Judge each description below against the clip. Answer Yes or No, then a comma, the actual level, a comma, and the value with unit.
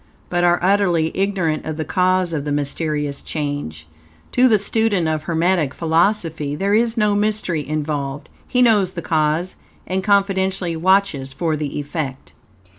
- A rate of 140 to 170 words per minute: Yes, average, 150 wpm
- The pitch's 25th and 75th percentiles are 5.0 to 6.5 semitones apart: No, average, 4.5 semitones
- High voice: No, medium, 170 Hz